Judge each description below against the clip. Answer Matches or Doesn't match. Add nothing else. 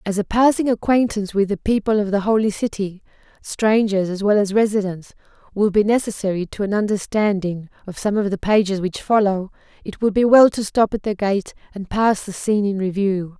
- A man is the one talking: Doesn't match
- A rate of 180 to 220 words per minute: Matches